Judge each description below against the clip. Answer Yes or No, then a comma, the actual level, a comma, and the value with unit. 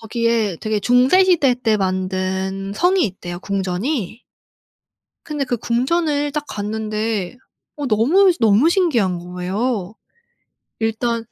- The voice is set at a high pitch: Yes, high, 225 Hz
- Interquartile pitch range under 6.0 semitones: Yes, wide, 5.5 semitones